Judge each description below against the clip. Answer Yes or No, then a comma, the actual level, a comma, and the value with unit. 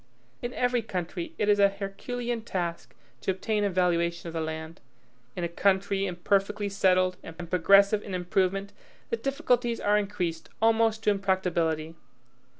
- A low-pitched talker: No, high, 195 Hz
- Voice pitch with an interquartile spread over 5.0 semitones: No, average, 3.1 semitones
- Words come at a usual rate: Yes, average, 150 wpm